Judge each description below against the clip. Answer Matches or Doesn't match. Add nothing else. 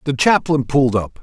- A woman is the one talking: Doesn't match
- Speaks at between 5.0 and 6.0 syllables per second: Matches